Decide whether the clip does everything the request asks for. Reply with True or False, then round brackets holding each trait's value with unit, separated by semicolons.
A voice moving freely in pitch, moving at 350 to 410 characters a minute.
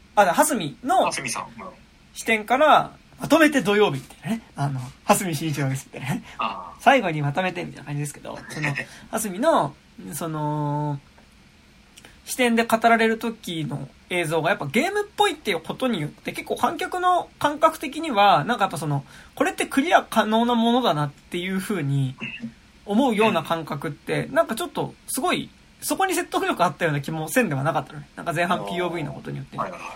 True (8.8 semitones; 365 characters per minute)